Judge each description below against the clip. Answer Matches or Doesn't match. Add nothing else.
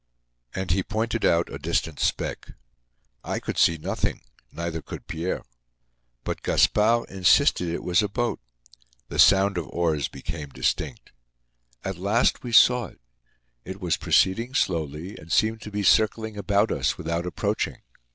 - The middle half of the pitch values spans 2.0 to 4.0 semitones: Doesn't match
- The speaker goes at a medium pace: Matches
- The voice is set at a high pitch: Doesn't match